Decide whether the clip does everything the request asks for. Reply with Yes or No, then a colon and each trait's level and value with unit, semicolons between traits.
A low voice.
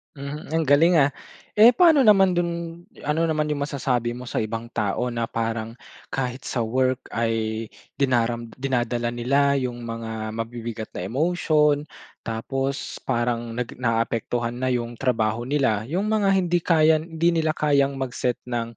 Yes: low, 125 Hz